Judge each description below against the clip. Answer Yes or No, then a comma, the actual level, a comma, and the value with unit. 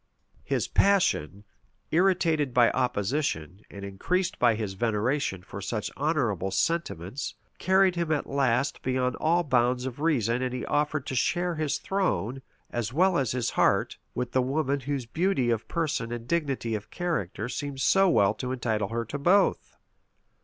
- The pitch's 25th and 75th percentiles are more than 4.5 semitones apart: Yes, wide, 5.4 semitones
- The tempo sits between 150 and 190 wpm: Yes, average, 160 wpm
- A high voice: No, low, 130 Hz